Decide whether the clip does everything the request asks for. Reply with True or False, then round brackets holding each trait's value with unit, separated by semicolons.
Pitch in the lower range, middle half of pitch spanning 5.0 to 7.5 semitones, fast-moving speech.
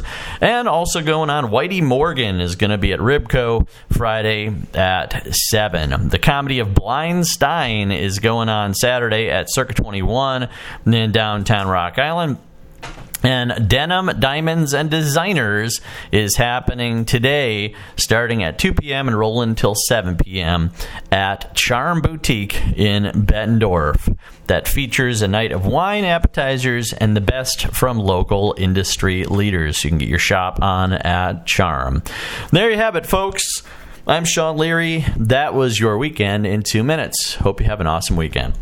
False (110 Hz; 5.5 semitones; 150 wpm)